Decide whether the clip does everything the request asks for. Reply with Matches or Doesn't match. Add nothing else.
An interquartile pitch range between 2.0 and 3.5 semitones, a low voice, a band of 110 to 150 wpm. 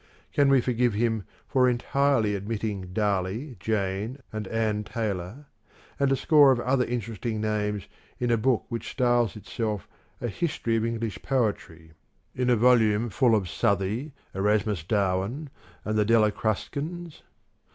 Matches